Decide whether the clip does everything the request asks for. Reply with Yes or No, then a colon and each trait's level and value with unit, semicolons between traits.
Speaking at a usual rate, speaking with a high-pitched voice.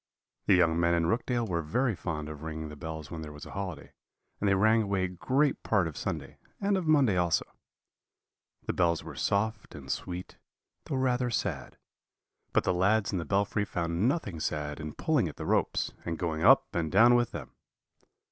No: average, 195 wpm; very low, 90 Hz